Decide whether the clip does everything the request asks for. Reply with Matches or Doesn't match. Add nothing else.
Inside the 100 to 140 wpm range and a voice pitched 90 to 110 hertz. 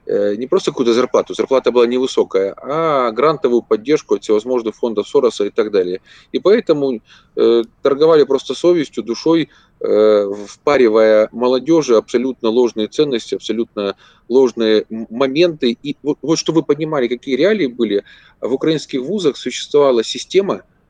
Doesn't match